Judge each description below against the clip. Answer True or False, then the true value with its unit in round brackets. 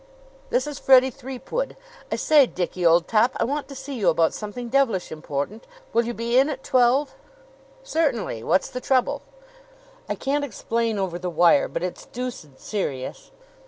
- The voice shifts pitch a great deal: True (6.7 semitones)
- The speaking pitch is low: False (235 Hz)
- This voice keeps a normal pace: True (165 wpm)